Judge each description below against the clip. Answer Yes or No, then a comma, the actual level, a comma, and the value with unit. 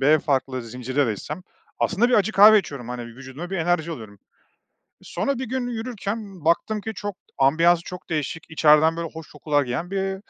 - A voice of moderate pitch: Yes, medium, 165 Hz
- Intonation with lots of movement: Yes, wide, 6.3 semitones